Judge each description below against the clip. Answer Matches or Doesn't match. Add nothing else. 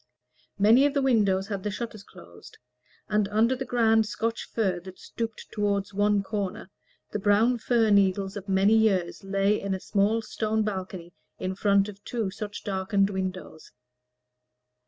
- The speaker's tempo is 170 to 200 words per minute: Doesn't match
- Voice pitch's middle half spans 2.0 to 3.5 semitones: Matches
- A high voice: Matches